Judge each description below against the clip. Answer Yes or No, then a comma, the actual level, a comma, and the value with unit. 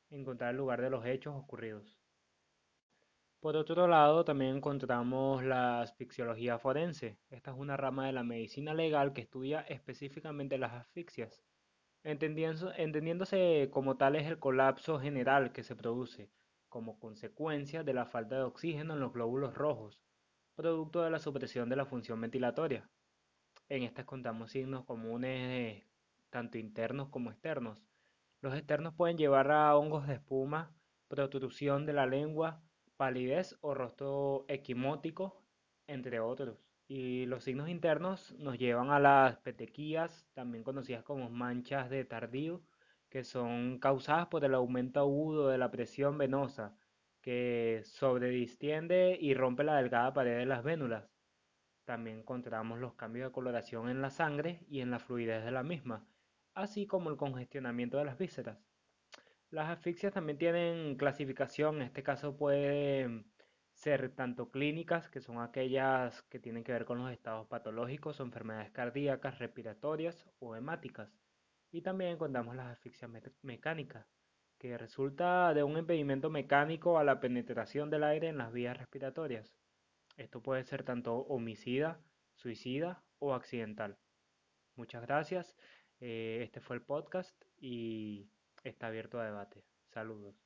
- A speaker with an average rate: Yes, average, 140 wpm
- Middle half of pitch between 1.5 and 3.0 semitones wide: No, average, 3.7 semitones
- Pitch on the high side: No, low, 135 Hz